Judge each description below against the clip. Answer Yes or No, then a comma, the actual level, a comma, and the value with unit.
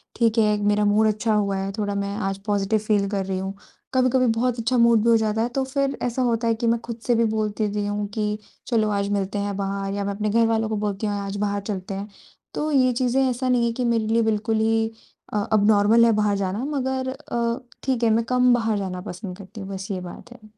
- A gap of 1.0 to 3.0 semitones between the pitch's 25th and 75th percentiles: Yes, narrow, 2.6 semitones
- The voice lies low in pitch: No, high, 215 Hz